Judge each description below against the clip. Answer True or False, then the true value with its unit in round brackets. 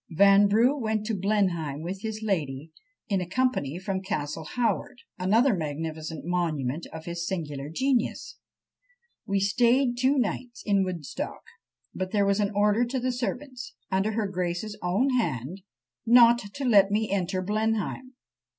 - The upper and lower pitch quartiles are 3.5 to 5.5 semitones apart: True (5.2 semitones)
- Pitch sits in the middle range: False (200 Hz)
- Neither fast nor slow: True (145 wpm)